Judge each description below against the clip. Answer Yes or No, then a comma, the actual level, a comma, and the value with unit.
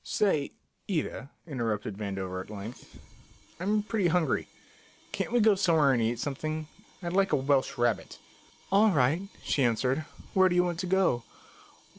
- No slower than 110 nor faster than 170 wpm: Yes, average, 155 wpm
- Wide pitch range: Yes, wide, 7.5 semitones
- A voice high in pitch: No, medium, 155 Hz